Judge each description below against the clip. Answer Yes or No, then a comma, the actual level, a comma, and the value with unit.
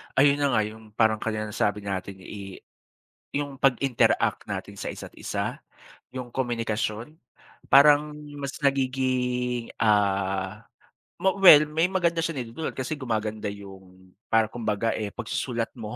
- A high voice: No, low, 115 Hz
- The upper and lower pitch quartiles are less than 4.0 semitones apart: No, average, 4.5 semitones